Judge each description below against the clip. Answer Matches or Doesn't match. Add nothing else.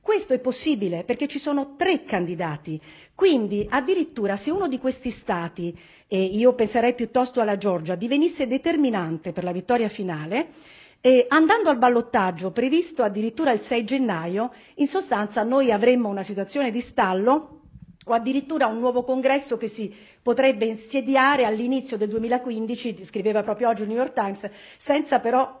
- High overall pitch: Matches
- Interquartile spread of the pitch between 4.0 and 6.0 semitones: Matches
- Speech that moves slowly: Doesn't match